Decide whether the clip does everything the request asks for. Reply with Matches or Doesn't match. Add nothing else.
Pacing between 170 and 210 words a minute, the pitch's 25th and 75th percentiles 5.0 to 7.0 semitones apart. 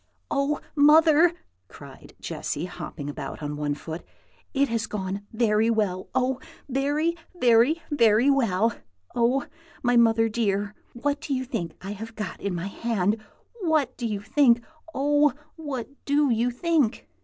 Doesn't match